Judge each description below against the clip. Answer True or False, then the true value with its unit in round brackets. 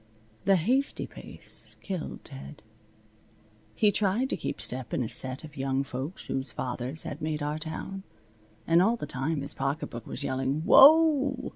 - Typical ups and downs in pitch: False (6.7 semitones)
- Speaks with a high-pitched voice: False (155 Hz)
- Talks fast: False (160 wpm)